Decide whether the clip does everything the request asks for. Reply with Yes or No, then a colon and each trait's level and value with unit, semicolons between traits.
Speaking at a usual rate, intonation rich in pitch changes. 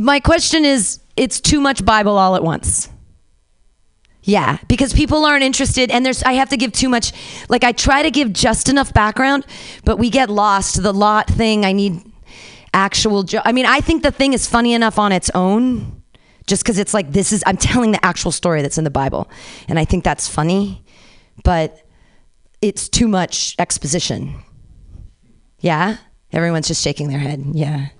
Yes: average, 185 wpm; wide, 6.5 semitones